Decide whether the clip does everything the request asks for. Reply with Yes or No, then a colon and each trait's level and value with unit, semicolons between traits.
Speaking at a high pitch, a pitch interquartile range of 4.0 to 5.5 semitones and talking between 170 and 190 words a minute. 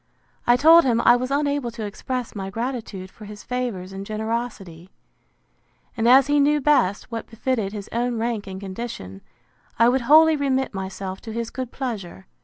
Yes: high, 235 Hz; average, 4.6 semitones; average, 175 wpm